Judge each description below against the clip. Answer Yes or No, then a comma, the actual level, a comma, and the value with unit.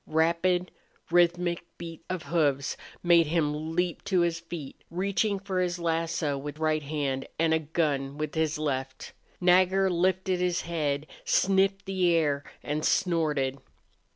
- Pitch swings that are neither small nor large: Yes, average, 3.1 semitones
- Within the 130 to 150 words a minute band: Yes, average, 140 wpm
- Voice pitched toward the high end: No, medium, 165 Hz